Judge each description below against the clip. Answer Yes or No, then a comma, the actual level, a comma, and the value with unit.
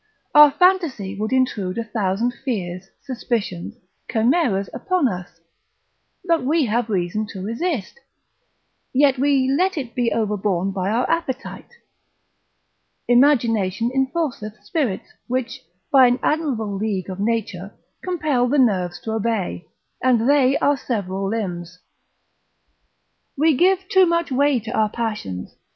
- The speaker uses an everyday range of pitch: No, wide, 5.8 semitones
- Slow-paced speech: Yes, slow, 125 wpm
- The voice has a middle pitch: No, high, 235 Hz